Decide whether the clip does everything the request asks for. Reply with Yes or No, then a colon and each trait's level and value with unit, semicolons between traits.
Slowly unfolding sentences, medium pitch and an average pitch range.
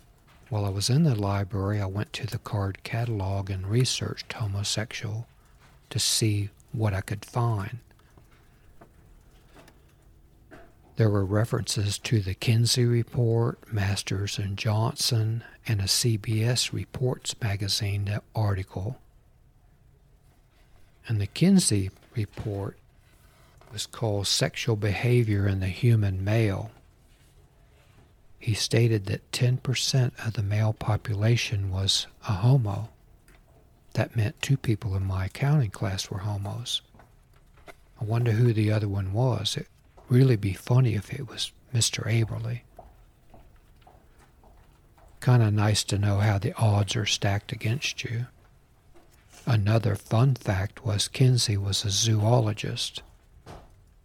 No: slow, 120 wpm; low, 110 Hz; average, 3.0 semitones